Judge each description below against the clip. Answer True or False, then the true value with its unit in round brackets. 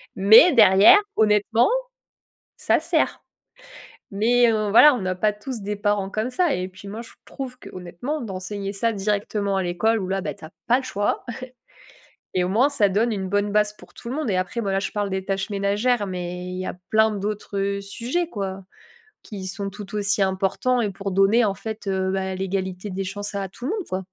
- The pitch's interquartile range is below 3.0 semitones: True (2.5 semitones)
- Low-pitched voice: False (200 Hz)